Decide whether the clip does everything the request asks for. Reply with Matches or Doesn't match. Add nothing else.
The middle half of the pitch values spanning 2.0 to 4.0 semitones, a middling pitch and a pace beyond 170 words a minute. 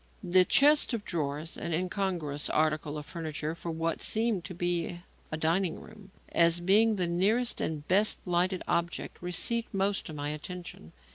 Doesn't match